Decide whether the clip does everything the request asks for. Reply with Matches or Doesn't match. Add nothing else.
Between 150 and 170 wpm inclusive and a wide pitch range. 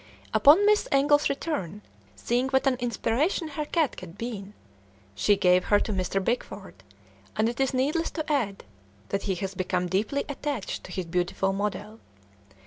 Matches